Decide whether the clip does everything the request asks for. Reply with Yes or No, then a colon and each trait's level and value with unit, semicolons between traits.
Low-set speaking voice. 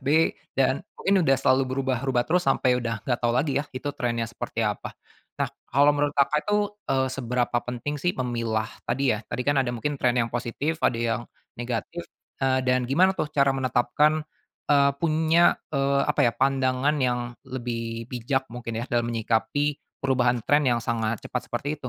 Yes: low, 130 Hz